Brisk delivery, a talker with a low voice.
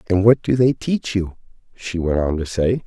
Yes: fast, 230 wpm; low, 100 Hz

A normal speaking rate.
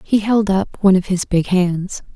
No: fast, 225 wpm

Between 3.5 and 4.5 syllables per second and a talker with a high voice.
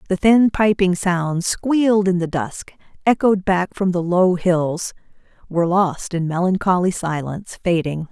No: 4.3 syllables/s; medium, 180 Hz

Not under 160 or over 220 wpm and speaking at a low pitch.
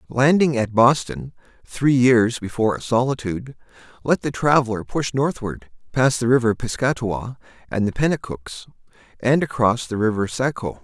No: average, 140 wpm; low, 120 Hz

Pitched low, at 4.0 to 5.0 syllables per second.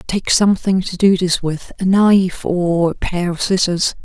No: medium, 185 Hz; 4.5 syllables/s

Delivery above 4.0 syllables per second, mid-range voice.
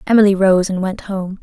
No: 5.3 syllables/s; high, 195 Hz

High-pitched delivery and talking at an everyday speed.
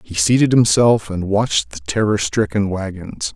No: low, 100 Hz; average, 160 wpm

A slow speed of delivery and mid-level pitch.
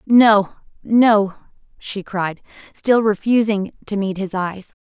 No: slow, 125 wpm; high, 205 Hz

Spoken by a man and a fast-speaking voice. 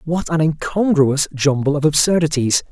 No: male; slow, 135 wpm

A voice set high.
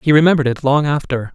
No: medium, 140 Hz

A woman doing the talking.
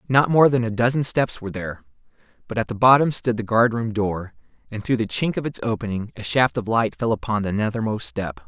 No: male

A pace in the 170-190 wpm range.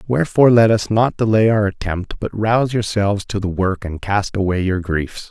No: fast, 205 wpm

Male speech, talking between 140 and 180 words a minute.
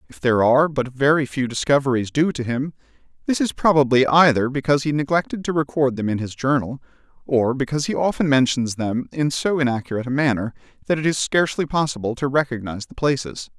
No: male; average, 190 wpm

